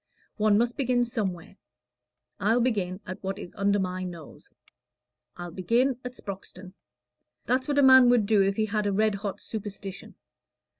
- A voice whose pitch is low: No, high, 205 Hz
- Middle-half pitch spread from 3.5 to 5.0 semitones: Yes, average, 3.9 semitones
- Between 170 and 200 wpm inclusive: No, average, 160 wpm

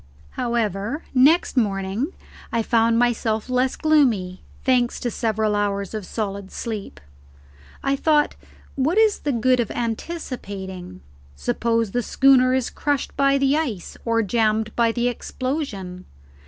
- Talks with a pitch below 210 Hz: No, high, 235 Hz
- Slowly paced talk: Yes, slow, 130 wpm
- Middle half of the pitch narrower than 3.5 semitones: No, average, 4.1 semitones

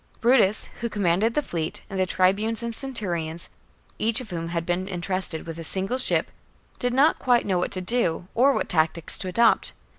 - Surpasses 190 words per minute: Yes, average, 200 wpm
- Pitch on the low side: No, high, 190 Hz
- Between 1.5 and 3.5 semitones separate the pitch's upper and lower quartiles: No, average, 5.3 semitones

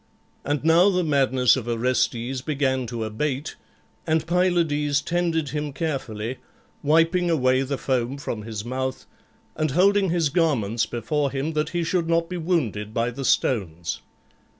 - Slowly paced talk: No, average, 150 wpm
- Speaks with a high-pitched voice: No, medium, 140 Hz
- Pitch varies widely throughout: No, average, 4.9 semitones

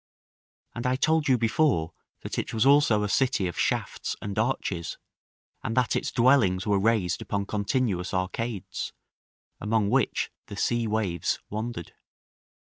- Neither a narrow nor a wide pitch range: Yes, average, 4.2 semitones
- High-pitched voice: No, low, 110 Hz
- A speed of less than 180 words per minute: Yes, average, 140 wpm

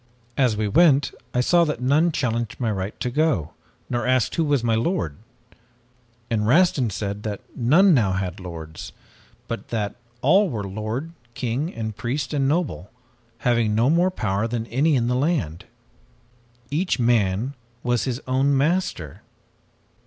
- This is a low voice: Yes, low, 120 Hz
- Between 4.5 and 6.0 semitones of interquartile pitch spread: Yes, average, 5.3 semitones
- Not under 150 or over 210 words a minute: Yes, average, 155 wpm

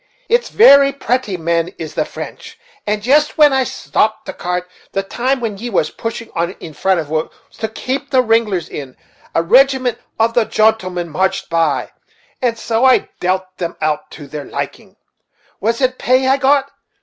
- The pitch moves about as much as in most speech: No, wide, 6.6 semitones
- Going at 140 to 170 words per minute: No, average, 180 wpm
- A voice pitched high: Yes, high, 220 Hz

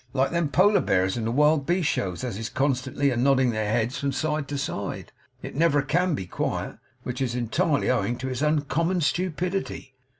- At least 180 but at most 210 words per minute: Yes, average, 195 wpm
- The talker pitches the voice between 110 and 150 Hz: Yes, medium, 140 Hz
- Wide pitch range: No, average, 4.3 semitones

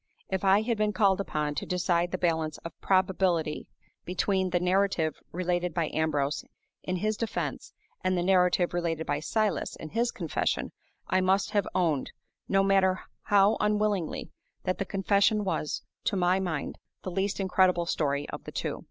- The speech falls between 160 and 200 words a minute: Yes, average, 165 wpm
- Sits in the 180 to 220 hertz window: Yes, medium, 185 Hz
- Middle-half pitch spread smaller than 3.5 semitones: Yes, narrow, 2.5 semitones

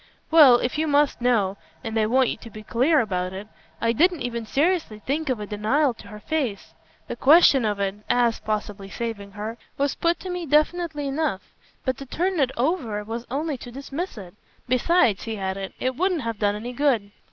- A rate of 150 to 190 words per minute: No, average, 200 wpm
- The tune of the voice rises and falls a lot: Yes, wide, 5.8 semitones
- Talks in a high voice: Yes, high, 245 Hz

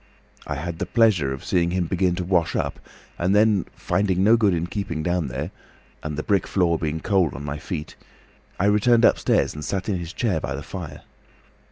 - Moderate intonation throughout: Yes, average, 3.8 semitones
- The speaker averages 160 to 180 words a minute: No, fast, 205 wpm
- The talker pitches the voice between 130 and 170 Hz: No, very low, 90 Hz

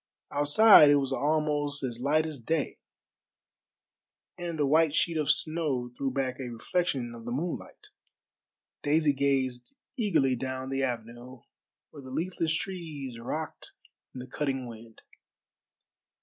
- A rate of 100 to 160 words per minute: Yes, slow, 135 wpm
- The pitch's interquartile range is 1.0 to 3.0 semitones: No, average, 3.5 semitones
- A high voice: No, medium, 140 Hz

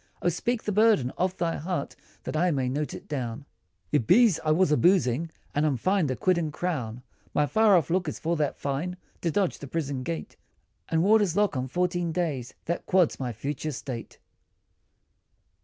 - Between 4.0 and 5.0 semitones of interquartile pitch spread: Yes, average, 4.7 semitones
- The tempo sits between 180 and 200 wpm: Yes, average, 190 wpm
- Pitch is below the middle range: No, medium, 160 Hz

